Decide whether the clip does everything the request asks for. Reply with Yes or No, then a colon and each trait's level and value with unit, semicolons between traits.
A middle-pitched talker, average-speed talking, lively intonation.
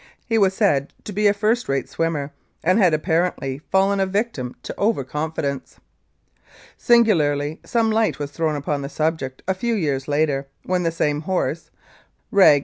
Yes: medium, 165 Hz; average, 165 wpm; wide, 5.7 semitones